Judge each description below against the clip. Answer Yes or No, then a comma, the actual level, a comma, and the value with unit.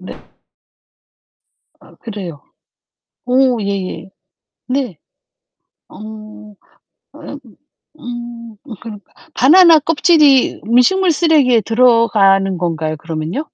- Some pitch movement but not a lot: No, wide, 5.9 semitones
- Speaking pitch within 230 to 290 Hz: Yes, high, 235 Hz